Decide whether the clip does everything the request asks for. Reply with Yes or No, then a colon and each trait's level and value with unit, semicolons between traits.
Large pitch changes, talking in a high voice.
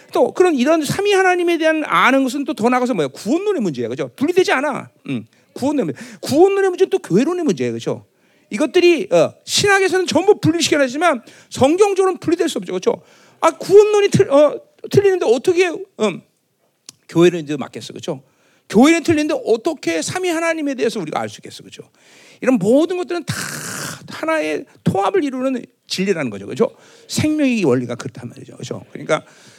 Yes: wide, 6.6 semitones; very high, 315 Hz